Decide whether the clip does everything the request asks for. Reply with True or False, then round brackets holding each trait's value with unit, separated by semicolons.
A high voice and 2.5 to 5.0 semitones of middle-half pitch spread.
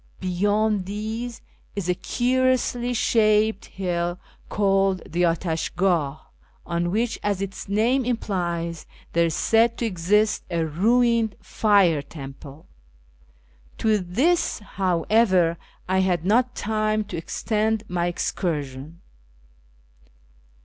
True (195 Hz; 4.3 semitones)